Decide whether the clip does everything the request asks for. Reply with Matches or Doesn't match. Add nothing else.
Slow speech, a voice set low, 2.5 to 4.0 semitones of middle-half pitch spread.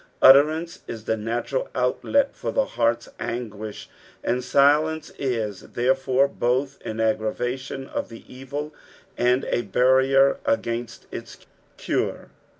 Matches